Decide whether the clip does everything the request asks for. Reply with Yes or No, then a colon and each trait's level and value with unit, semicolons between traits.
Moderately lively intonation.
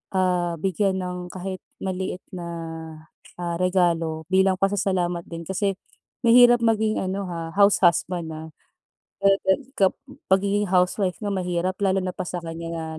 No: narrow, 2.0 semitones